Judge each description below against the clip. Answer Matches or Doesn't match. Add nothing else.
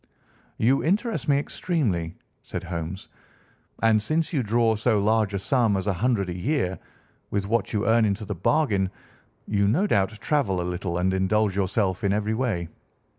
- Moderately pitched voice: Doesn't match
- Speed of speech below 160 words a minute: Doesn't match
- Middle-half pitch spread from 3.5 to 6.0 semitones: Matches